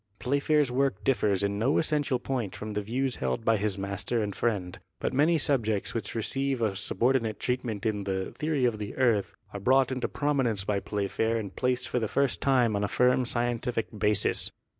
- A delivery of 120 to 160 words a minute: No, average, 190 wpm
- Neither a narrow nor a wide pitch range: Yes, average, 4.1 semitones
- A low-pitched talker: Yes, low, 115 Hz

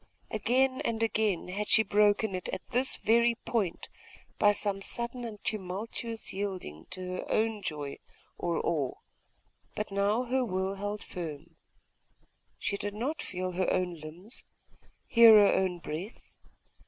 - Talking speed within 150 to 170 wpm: No, average, 140 wpm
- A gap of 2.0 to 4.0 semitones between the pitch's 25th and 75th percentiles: Yes, average, 3.6 semitones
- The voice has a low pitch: No, high, 205 Hz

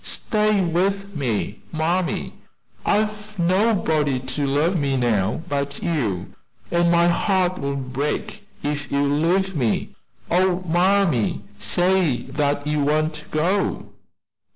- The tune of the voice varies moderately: Yes, average, 4.9 semitones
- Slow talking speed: Yes, slow, 115 wpm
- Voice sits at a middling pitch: Yes, medium, 160 Hz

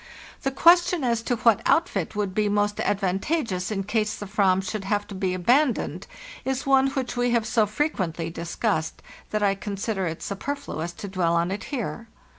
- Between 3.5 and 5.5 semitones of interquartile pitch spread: Yes, average, 4.4 semitones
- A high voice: Yes, high, 210 Hz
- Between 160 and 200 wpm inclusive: Yes, average, 180 wpm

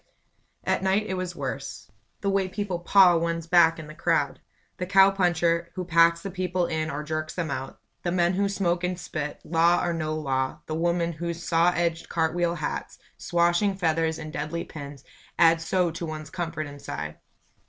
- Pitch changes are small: Yes, narrow, 2.2 semitones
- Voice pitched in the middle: Yes, medium, 170 Hz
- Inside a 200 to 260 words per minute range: No, average, 185 wpm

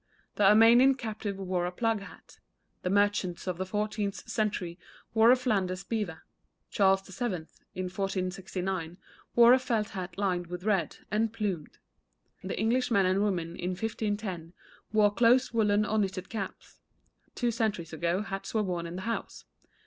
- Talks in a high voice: Yes, high, 200 Hz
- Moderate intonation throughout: Yes, average, 3.1 semitones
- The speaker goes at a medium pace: Yes, average, 155 wpm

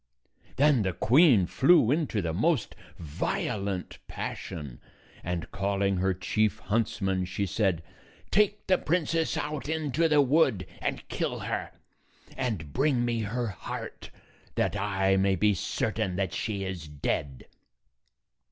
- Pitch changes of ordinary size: No, wide, 7.1 semitones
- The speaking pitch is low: Yes, low, 105 Hz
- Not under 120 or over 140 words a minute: Yes, slow, 135 wpm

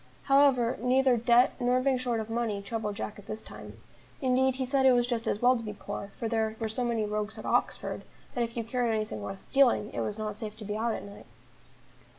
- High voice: Yes, high, 230 Hz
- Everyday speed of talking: No, fast, 235 wpm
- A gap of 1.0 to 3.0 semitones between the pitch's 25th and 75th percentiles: Yes, average, 2.7 semitones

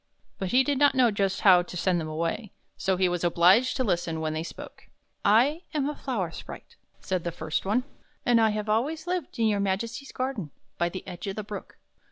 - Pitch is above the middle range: Yes, high, 200 Hz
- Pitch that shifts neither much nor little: No, wide, 6.3 semitones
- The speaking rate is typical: No, fast, 225 wpm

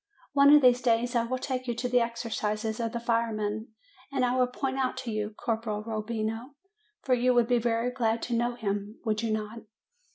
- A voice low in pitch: No, high, 235 Hz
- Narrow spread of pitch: Yes, narrow, 2.2 semitones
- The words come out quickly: Yes, fast, 215 wpm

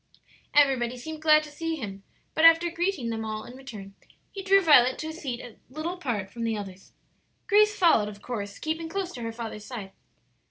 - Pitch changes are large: Yes, wide, 6.6 semitones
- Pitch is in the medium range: No, very high, 260 Hz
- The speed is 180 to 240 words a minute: Yes, average, 200 wpm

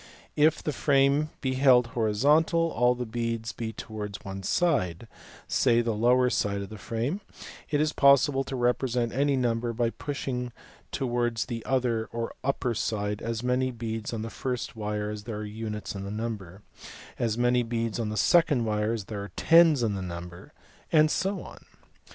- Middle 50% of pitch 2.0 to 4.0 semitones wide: Yes, average, 3.5 semitones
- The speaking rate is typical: Yes, average, 180 wpm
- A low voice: Yes, low, 115 Hz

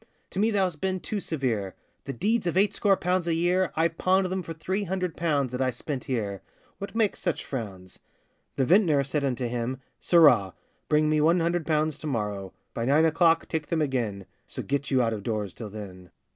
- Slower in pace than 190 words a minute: No, average, 200 wpm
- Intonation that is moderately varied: No, wide, 6.7 semitones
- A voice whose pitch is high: No, medium, 150 Hz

